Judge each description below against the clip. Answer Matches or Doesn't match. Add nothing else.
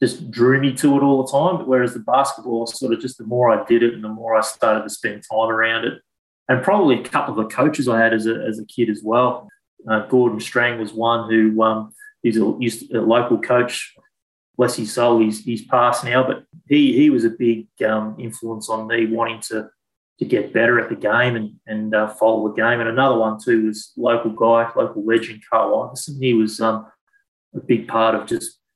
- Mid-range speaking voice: Doesn't match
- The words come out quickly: Matches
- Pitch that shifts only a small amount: Matches